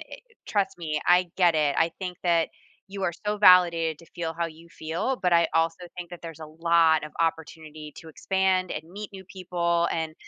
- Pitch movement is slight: Yes, narrow, 2.1 semitones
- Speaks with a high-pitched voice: No, medium, 170 Hz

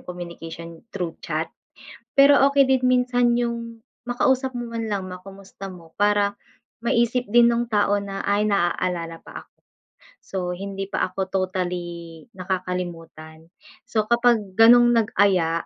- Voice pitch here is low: No, high, 200 Hz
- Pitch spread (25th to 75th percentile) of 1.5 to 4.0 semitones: No, average, 5.0 semitones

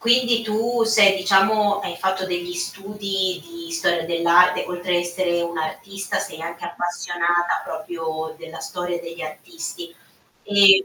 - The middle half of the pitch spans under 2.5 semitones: No, average, 2.9 semitones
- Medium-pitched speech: Yes, medium, 180 Hz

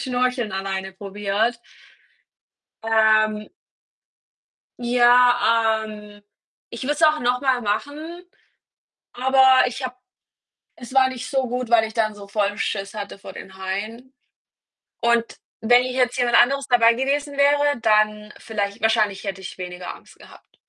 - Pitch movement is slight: No, average, 3.3 semitones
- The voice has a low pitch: No, high, 230 Hz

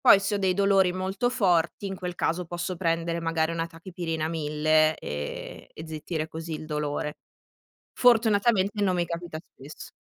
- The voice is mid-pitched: Yes, medium, 170 Hz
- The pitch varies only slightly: No, average, 3.3 semitones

